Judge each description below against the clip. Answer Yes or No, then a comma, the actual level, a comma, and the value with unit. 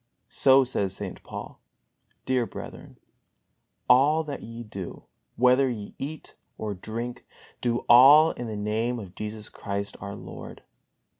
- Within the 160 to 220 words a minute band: No, slow, 135 wpm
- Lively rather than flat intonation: No, average, 3.7 semitones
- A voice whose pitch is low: Yes, low, 120 Hz